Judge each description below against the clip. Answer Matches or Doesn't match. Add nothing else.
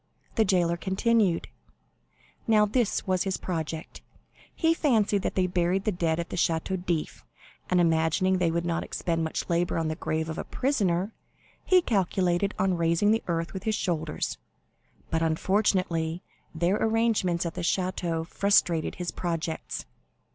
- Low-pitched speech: Doesn't match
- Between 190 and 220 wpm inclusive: Doesn't match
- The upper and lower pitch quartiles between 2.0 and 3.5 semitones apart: Matches